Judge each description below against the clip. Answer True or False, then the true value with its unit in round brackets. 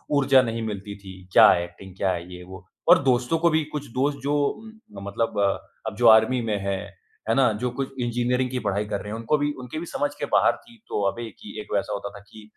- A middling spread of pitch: True (4.5 semitones)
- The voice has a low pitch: True (115 Hz)